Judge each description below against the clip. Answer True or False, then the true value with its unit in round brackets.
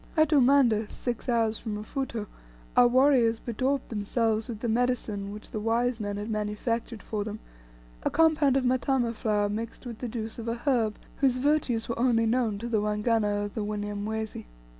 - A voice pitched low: False (230 Hz)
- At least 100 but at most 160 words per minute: False (180 wpm)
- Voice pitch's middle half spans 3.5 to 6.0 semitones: False (2.7 semitones)